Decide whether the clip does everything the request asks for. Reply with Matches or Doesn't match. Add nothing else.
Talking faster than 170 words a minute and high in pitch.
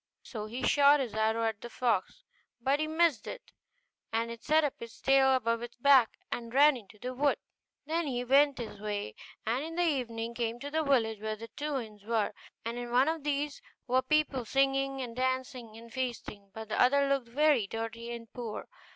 Matches